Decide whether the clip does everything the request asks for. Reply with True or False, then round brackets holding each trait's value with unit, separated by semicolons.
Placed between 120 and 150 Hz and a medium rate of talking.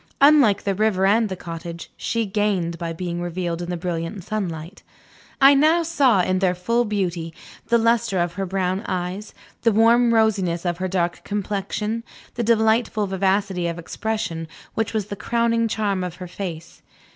False (195 Hz; 170 wpm)